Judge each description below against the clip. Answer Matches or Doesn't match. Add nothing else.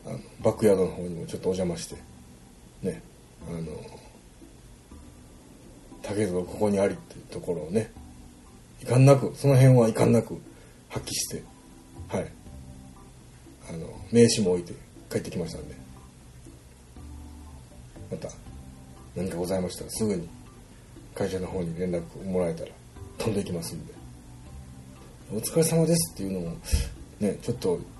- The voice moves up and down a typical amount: Doesn't match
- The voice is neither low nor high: Doesn't match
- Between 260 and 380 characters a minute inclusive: Matches